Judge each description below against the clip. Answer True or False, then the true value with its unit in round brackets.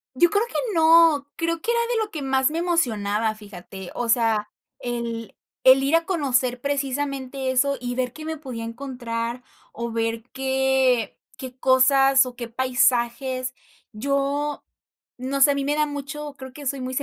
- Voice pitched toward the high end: True (265 Hz)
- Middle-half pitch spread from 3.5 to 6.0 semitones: False (3.0 semitones)